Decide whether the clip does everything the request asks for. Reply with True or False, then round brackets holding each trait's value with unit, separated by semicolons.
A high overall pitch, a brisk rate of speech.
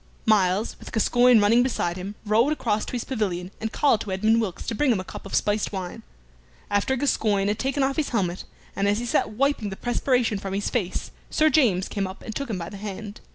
True (215 Hz; 230 wpm)